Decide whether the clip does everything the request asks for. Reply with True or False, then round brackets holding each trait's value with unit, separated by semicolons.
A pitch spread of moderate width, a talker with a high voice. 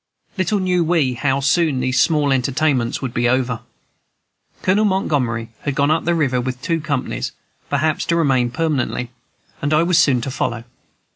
False (4.5 semitones; 140 Hz)